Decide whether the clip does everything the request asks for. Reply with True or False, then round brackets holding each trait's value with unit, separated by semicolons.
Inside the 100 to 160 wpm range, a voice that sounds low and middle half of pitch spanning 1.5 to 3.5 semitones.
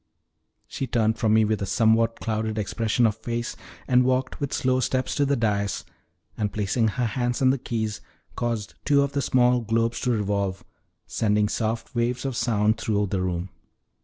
False (180 wpm; 115 Hz; 2.8 semitones)